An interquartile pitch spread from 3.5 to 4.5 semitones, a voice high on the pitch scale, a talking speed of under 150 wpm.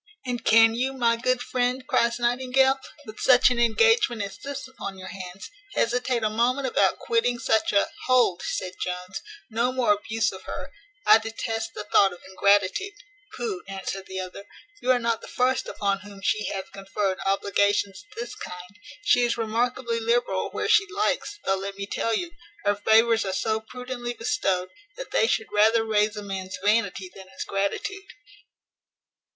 No: average, 3.9 semitones; high, 225 Hz; average, 175 wpm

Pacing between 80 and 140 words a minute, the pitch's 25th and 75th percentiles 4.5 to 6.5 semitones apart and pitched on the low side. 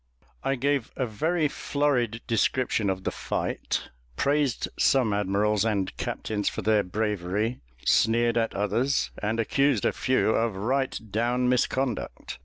No: slow, 135 wpm; average, 3.8 semitones; low, 115 Hz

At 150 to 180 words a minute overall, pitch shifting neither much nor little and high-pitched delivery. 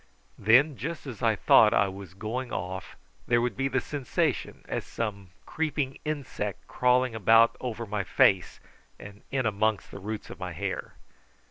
No: average, 165 wpm; average, 4.2 semitones; low, 115 Hz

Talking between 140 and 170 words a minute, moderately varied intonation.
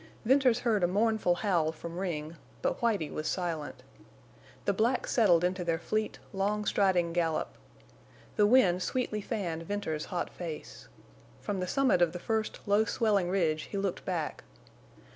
Yes: average, 155 wpm; average, 4.0 semitones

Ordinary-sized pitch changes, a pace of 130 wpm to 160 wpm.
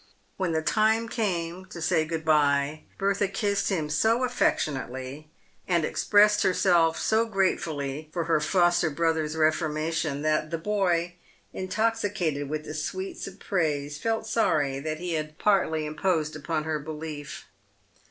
Yes: average, 4.0 semitones; average, 140 wpm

